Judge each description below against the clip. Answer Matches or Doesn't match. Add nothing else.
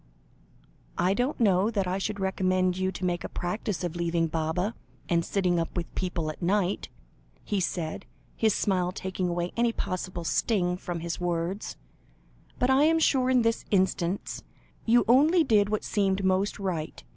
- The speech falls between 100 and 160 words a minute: Doesn't match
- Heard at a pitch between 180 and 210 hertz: Matches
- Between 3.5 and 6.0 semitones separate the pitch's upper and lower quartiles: Doesn't match